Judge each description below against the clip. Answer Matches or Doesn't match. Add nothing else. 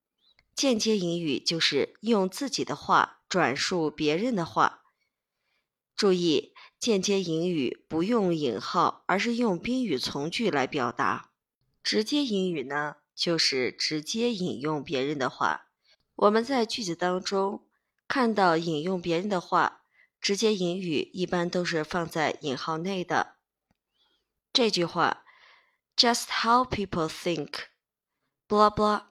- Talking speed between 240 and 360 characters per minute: Doesn't match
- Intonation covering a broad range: Doesn't match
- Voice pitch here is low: Doesn't match